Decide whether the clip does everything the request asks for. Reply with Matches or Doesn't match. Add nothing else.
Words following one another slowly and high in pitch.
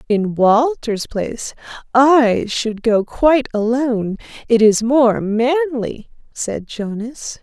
Matches